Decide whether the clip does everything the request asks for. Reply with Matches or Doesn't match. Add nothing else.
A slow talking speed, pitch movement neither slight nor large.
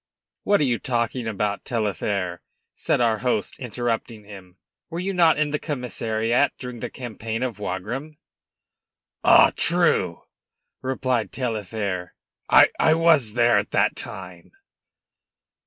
Matches